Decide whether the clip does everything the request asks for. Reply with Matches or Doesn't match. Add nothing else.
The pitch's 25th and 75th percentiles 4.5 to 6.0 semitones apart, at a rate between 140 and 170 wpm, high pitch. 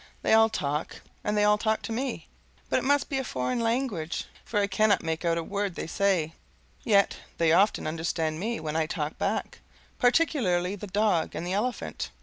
Doesn't match